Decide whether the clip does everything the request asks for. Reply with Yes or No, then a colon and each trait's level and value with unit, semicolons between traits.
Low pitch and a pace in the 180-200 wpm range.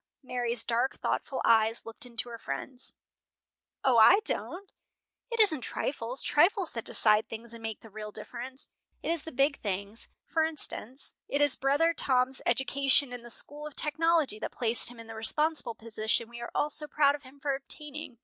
No: very high, 260 Hz; average, 185 wpm